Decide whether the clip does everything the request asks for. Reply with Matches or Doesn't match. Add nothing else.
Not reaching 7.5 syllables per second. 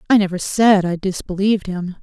Matches